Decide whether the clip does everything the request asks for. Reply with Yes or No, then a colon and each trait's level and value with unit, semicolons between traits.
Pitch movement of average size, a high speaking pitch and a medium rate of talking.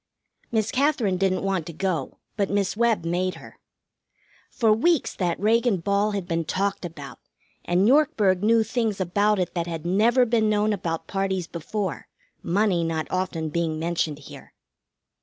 Yes: average, 3.9 semitones; high, 195 Hz; average, 160 wpm